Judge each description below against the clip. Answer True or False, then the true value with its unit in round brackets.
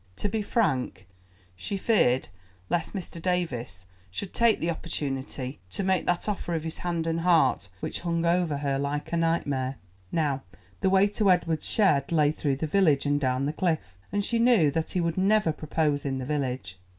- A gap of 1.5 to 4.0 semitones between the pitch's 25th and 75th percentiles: False (4.6 semitones)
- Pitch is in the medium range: True (160 Hz)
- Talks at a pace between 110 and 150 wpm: False (185 wpm)